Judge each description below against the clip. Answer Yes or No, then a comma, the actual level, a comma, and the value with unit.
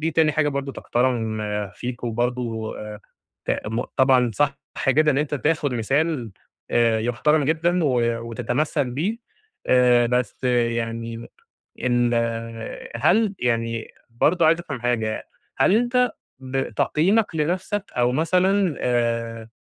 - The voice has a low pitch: Yes, low, 130 Hz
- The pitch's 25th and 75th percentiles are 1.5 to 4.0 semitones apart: No, average, 5.0 semitones